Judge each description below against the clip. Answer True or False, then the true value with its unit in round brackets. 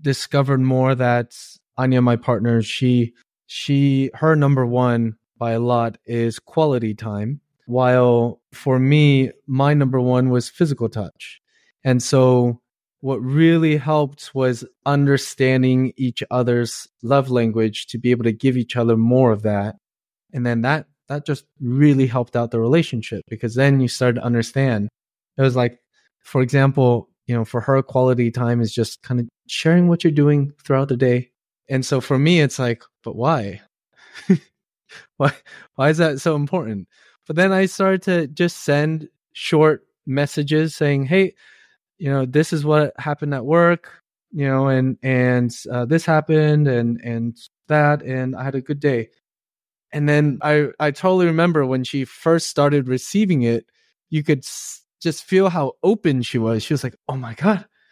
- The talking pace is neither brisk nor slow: True (165 wpm)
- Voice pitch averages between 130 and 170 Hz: True (135 Hz)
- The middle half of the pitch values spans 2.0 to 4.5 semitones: True (3.7 semitones)